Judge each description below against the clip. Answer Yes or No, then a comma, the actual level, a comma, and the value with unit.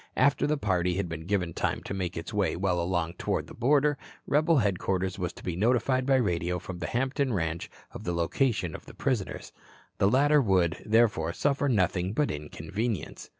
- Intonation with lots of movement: Yes, wide, 6.7 semitones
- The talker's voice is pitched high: No, very low, 95 Hz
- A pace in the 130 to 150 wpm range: No, average, 190 wpm